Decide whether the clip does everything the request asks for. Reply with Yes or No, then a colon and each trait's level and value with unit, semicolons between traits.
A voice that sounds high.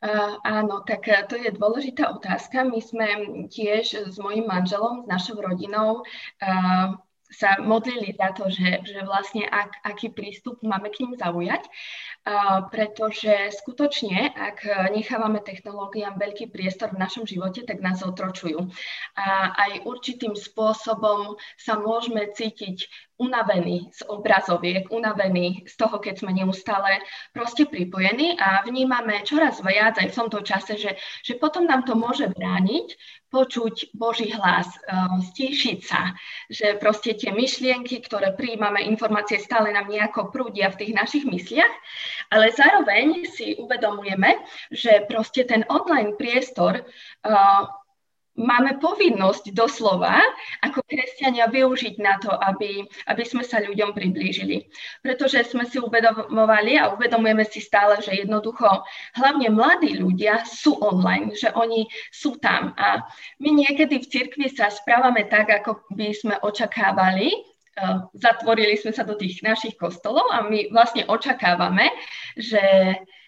Yes: high, 215 Hz